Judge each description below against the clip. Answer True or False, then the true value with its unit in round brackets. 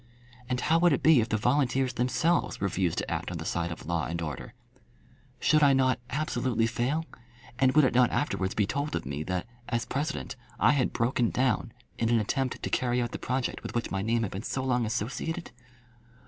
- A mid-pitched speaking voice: False (125 Hz)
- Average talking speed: False (210 wpm)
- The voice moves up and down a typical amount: True (3.7 semitones)